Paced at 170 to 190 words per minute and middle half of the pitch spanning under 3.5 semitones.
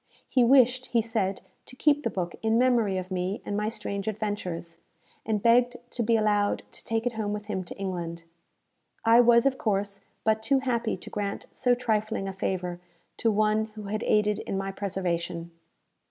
Yes: average, 185 wpm; average, 3.1 semitones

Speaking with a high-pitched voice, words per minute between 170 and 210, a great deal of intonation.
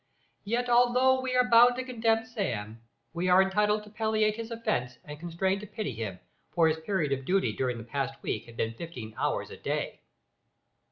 Yes: high, 195 Hz; average, 190 wpm; wide, 8.9 semitones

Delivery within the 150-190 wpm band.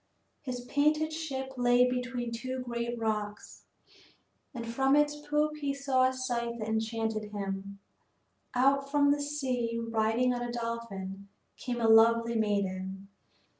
No: slow, 135 wpm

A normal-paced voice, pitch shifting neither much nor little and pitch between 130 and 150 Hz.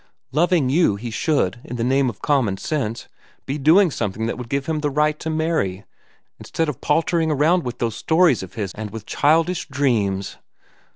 No: average, 185 wpm; wide, 5.8 semitones; medium, 140 Hz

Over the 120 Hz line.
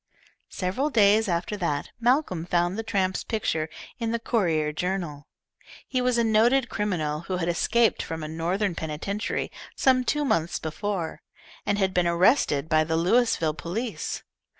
Yes: medium, 185 Hz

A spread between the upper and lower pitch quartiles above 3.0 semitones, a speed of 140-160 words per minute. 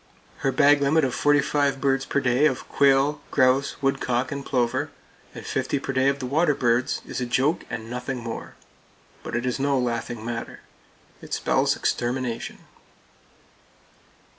No: narrow, 2.4 semitones; average, 155 wpm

